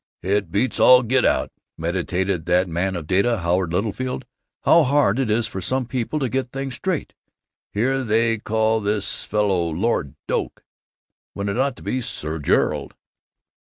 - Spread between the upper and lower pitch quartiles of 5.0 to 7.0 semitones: Yes, wide, 5.4 semitones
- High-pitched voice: No, low, 105 Hz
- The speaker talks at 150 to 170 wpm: Yes, average, 160 wpm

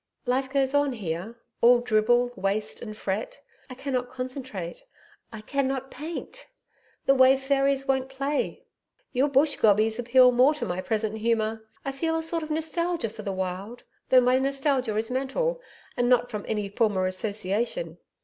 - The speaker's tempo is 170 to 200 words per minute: No, average, 160 wpm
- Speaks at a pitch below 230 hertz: No, very high, 250 Hz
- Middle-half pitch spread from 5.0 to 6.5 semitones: No, average, 4.0 semitones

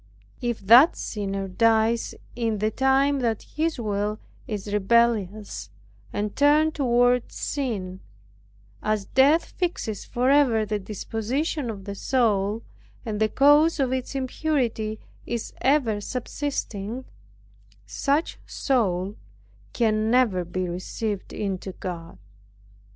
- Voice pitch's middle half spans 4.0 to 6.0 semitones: Yes, average, 4.4 semitones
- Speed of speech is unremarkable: No, slow, 110 wpm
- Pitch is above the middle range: Yes, high, 225 Hz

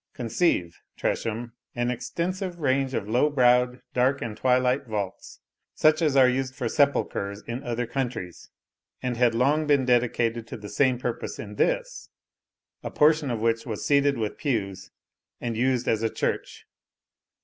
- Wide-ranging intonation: No, average, 3.4 semitones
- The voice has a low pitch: Yes, low, 125 Hz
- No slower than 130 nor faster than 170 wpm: Yes, average, 155 wpm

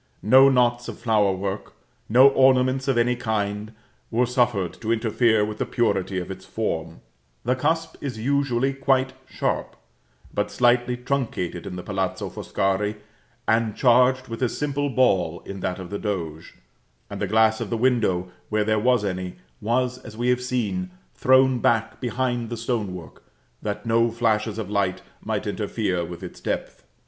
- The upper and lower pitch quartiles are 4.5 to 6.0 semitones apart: No, average, 3.8 semitones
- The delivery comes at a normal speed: Yes, average, 165 wpm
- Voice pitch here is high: No, low, 115 Hz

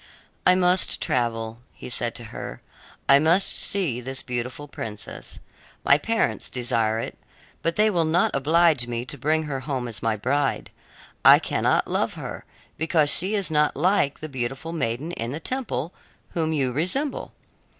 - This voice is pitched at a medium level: Yes, medium, 145 Hz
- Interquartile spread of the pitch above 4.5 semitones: Yes, wide, 5.5 semitones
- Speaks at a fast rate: No, average, 165 wpm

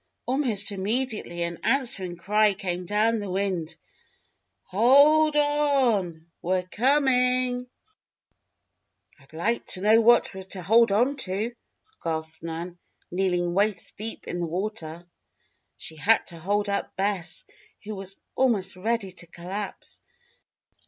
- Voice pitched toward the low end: No, high, 200 Hz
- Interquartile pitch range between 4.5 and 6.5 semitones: Yes, average, 4.9 semitones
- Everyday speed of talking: No, slow, 125 wpm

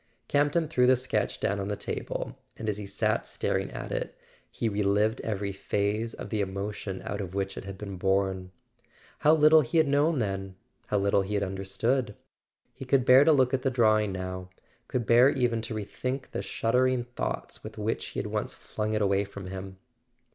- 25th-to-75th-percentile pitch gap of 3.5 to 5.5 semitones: Yes, average, 4.5 semitones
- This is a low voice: Yes, low, 105 Hz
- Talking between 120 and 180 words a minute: No, average, 200 wpm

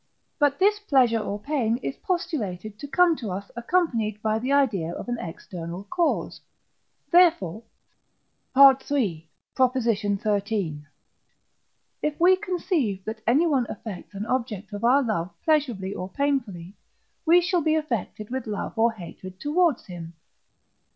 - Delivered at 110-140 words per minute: Yes, slow, 135 wpm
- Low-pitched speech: No, high, 235 Hz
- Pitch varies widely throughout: Yes, wide, 6.5 semitones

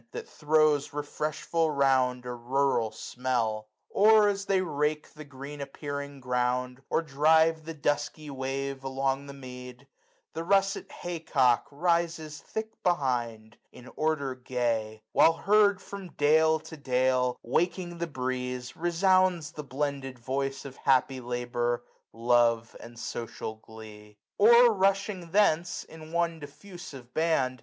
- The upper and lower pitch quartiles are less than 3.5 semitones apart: No, average, 4.5 semitones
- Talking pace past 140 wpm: No, slow, 135 wpm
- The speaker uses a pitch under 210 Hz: Yes, medium, 140 Hz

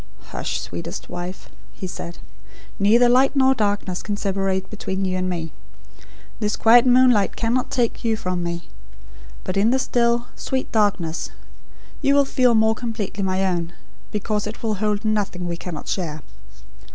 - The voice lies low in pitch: No, high, 205 Hz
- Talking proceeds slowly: No, average, 155 wpm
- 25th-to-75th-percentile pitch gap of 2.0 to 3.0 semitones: No, average, 4.3 semitones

